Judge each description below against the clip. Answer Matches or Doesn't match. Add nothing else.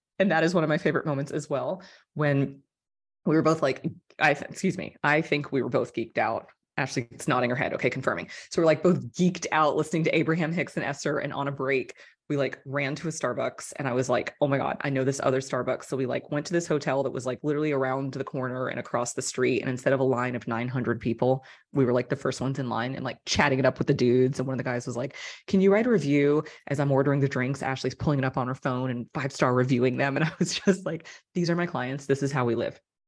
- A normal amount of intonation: Matches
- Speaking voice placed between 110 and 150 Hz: Matches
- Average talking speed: Doesn't match